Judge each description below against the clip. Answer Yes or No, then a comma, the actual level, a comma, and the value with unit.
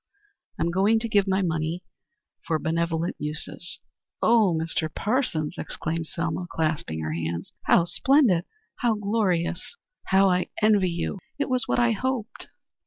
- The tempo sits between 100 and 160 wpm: Yes, average, 140 wpm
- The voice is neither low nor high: Yes, medium, 180 Hz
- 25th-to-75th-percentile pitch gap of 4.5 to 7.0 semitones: Yes, average, 4.9 semitones